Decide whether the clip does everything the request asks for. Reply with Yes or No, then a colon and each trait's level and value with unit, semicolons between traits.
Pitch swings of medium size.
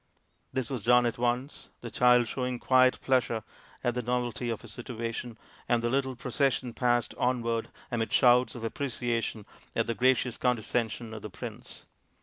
No: narrow, 1.5 semitones